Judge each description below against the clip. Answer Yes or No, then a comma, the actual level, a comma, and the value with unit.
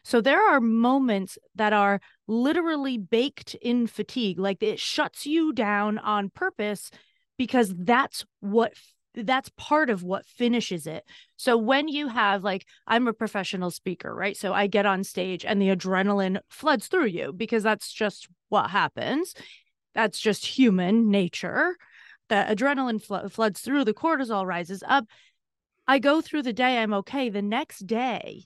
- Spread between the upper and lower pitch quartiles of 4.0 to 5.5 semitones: Yes, average, 4.7 semitones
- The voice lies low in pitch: No, high, 220 Hz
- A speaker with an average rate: Yes, average, 160 wpm